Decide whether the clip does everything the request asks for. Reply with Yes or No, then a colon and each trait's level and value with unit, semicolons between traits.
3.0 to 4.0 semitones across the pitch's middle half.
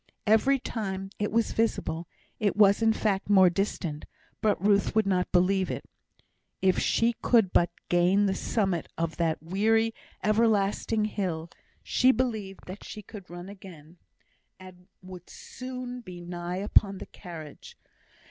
Yes: average, 3.4 semitones